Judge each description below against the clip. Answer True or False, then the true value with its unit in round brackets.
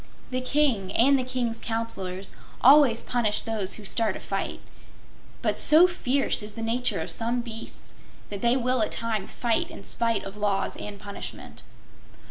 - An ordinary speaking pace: True (165 wpm)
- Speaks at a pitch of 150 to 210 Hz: False (230 Hz)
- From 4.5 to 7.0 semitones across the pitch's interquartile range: False (3.3 semitones)